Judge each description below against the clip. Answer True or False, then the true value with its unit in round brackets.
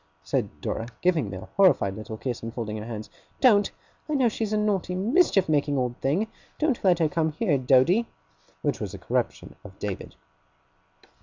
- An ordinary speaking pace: True (180 wpm)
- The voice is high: False (155 Hz)